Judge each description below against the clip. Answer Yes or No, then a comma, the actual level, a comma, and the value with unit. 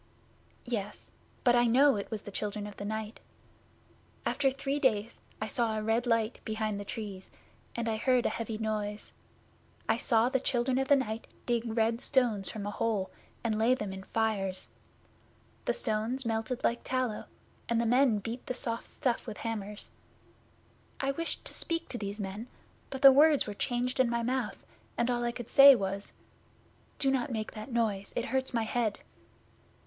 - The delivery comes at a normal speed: Yes, average, 180 wpm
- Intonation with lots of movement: No, average, 2.8 semitones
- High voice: Yes, high, 230 Hz